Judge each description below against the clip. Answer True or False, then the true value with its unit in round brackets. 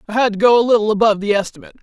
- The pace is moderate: False (295 wpm)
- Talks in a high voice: True (215 Hz)